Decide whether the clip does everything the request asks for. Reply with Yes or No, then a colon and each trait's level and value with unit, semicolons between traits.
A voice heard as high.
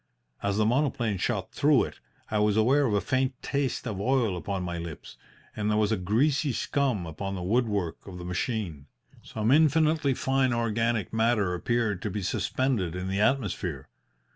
No: low, 110 Hz